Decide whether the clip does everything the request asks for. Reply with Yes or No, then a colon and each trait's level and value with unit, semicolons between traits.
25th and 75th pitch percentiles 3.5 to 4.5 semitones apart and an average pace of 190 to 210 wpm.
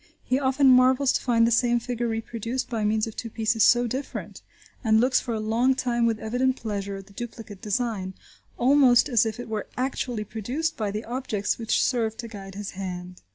No: average, 2.7 semitones; average, 200 wpm